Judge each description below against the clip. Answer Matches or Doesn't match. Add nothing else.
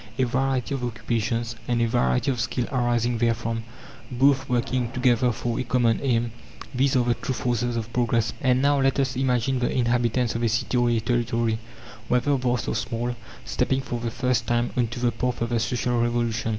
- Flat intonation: Matches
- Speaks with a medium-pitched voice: Doesn't match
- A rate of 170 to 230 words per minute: Matches